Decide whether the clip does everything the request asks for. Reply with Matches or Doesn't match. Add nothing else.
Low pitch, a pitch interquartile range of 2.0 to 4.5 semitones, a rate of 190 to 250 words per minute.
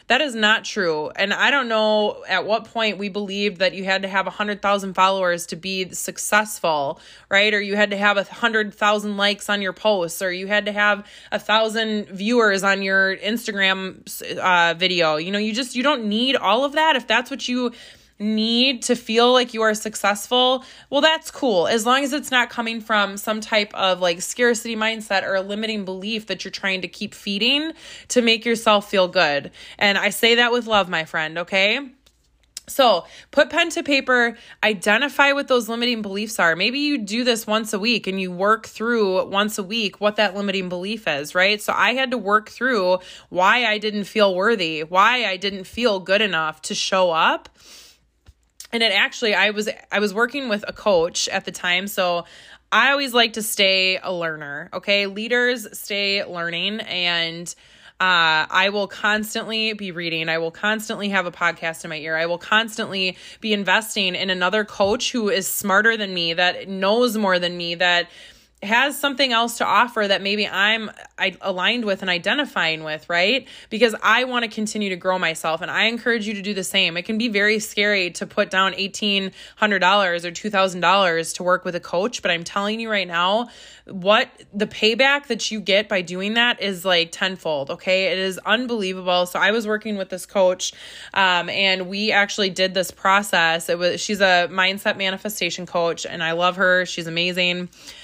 Doesn't match